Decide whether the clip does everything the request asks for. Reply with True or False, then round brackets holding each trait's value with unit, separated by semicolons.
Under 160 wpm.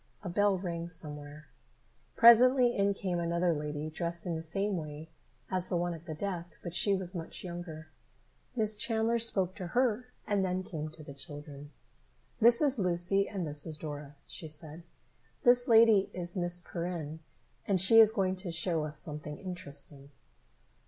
False (170 wpm)